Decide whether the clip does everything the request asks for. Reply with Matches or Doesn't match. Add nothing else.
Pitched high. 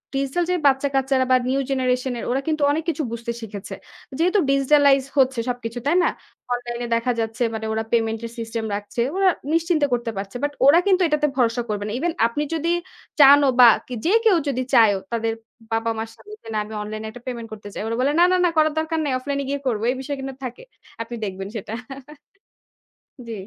Matches